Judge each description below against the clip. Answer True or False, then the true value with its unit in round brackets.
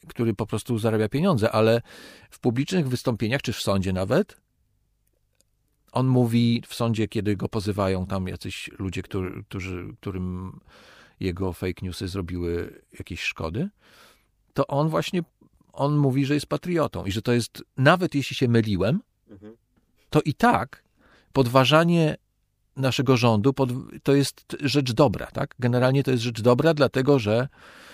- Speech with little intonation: False (5.2 semitones)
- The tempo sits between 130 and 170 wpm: True (140 wpm)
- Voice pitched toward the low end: True (120 Hz)